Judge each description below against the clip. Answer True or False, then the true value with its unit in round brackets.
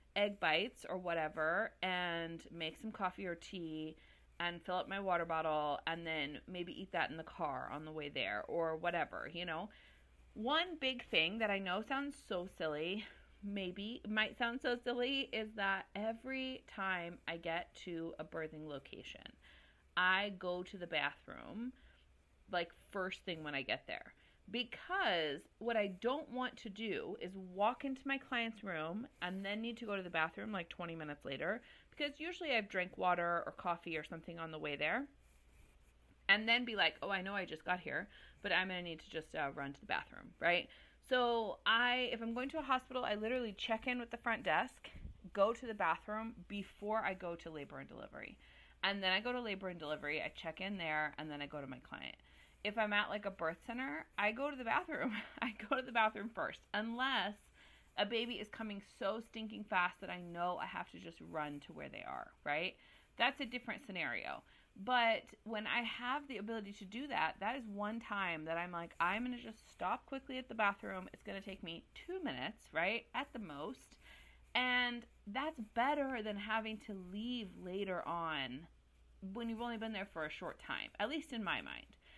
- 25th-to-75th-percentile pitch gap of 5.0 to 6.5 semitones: True (5.6 semitones)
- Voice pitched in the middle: False (200 Hz)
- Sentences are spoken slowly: False (205 wpm)